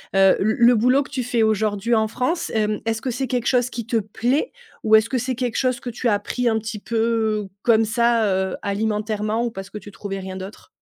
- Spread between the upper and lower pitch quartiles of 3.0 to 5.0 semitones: No, narrow, 2.5 semitones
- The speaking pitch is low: No, high, 225 Hz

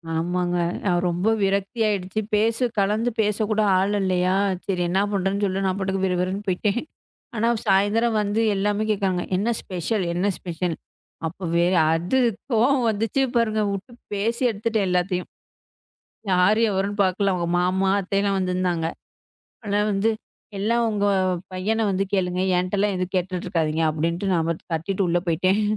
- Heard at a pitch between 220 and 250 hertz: No, high, 195 Hz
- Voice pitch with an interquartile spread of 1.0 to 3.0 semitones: Yes, narrow, 2.5 semitones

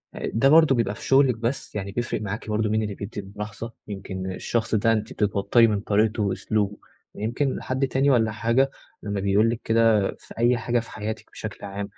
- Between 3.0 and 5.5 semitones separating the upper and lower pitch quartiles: No, narrow, 2.5 semitones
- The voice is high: No, low, 110 Hz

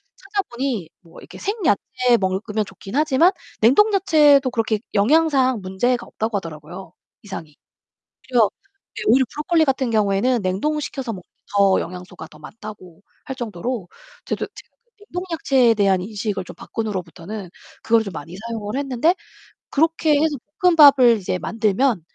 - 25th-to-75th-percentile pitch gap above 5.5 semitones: Yes, wide, 6.3 semitones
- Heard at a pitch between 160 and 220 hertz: No, high, 230 Hz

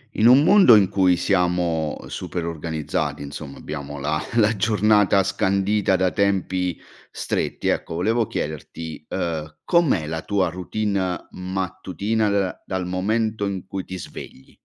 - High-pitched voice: No, very low, 95 Hz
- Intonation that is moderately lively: Yes, average, 4.0 semitones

